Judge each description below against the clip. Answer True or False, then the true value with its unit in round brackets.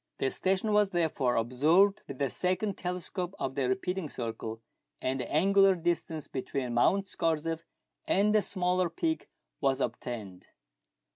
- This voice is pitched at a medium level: True (165 Hz)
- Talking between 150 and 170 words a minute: False (140 wpm)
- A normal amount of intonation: False (6.5 semitones)